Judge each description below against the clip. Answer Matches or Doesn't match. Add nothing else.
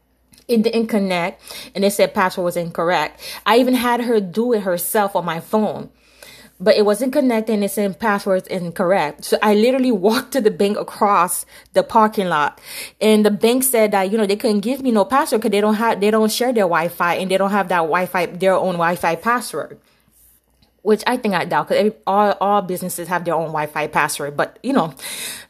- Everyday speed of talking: Doesn't match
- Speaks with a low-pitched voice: Doesn't match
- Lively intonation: Doesn't match